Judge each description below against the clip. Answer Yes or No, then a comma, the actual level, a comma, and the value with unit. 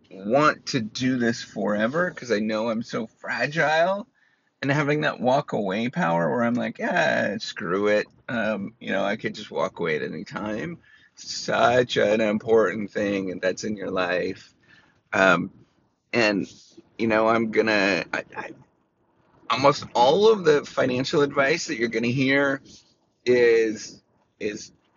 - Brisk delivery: No, average, 150 wpm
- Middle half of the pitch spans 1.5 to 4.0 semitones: No, average, 4.6 semitones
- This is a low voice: Yes, low, 115 Hz